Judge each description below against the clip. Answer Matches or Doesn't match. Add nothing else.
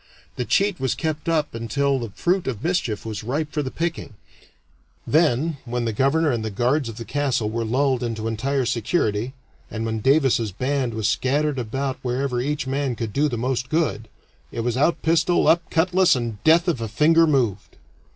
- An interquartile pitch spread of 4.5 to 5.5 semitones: Matches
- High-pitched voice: Doesn't match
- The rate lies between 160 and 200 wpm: Matches